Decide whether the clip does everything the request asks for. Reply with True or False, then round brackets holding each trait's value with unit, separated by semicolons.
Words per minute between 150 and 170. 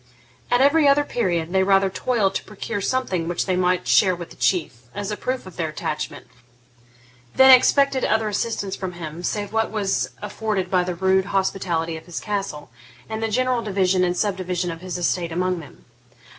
False (185 wpm)